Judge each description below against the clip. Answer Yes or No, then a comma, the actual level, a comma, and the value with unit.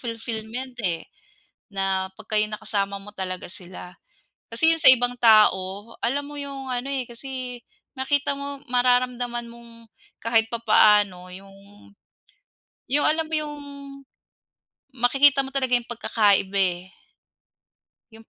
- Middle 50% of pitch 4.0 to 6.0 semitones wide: Yes, average, 4.4 semitones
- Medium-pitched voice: No, high, 235 Hz